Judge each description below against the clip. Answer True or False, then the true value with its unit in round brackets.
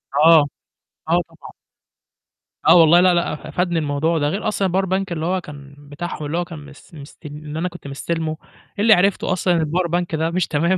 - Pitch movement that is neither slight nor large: True (3.2 semitones)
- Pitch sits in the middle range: True (165 Hz)